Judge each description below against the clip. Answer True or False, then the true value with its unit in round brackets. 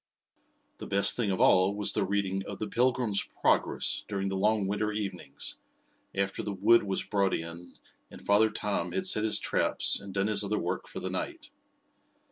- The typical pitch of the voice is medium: False (100 Hz)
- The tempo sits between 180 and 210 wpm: True (185 wpm)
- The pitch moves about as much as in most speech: False (1.7 semitones)